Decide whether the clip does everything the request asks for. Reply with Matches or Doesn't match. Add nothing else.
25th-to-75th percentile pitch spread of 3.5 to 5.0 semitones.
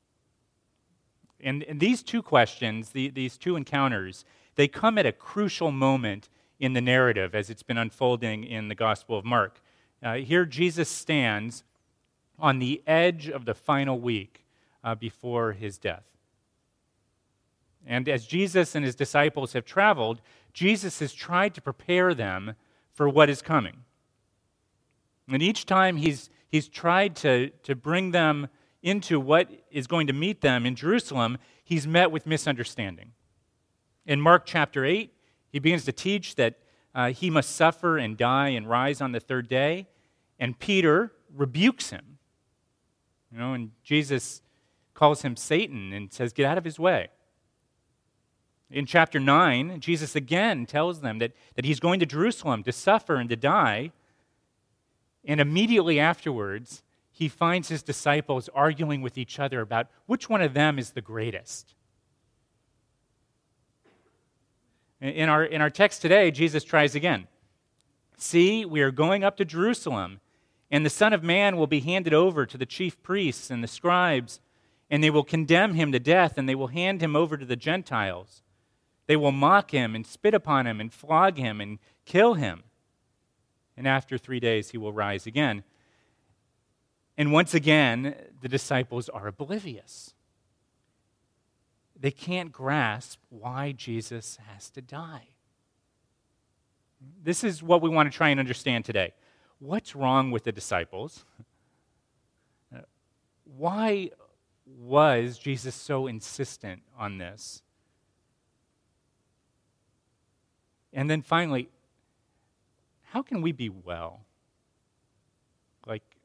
Doesn't match